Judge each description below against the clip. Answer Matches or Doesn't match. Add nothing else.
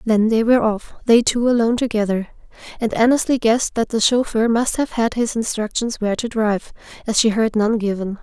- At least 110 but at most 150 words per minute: Doesn't match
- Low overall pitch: Doesn't match